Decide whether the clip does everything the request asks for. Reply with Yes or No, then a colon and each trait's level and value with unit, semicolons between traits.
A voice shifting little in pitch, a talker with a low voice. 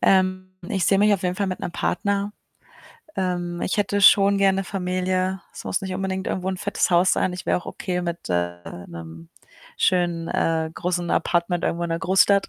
No: narrow, 1.9 semitones; medium, 185 Hz